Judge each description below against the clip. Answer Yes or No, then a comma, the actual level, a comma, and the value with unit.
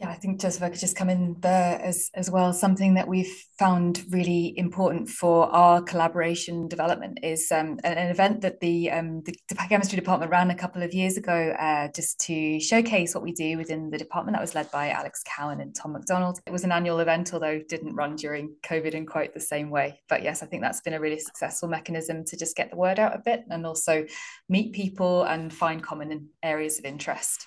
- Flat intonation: Yes, narrow, 2.3 semitones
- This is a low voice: No, medium, 170 Hz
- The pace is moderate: No, fast, 225 wpm